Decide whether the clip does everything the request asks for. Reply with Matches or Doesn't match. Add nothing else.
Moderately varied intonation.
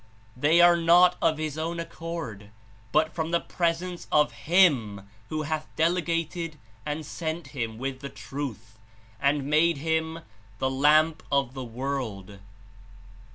Matches